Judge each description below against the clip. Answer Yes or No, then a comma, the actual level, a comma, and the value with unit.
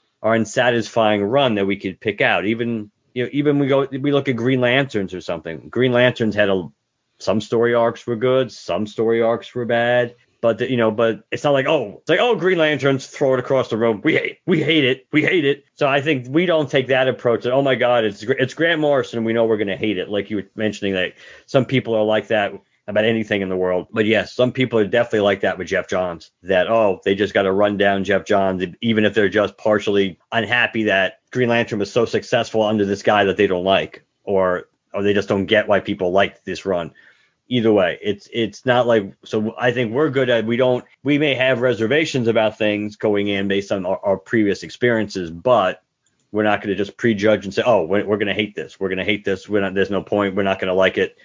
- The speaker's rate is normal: No, fast, 245 wpm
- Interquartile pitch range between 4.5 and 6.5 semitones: No, average, 3.9 semitones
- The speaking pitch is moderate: No, low, 115 Hz